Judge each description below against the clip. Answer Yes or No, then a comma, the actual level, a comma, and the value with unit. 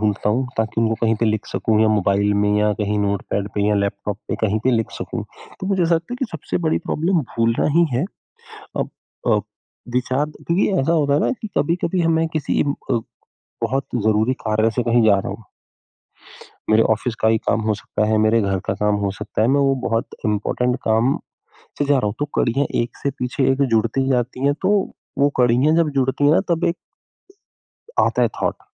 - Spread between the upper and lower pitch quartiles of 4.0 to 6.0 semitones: Yes, average, 4.9 semitones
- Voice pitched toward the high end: No, low, 120 Hz